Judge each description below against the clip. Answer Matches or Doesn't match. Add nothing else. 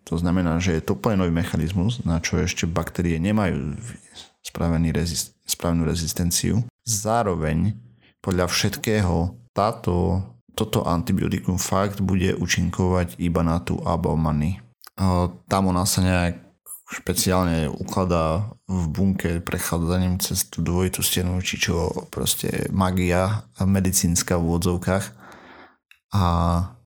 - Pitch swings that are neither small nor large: Doesn't match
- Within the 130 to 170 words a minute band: Doesn't match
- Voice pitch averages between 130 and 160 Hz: Doesn't match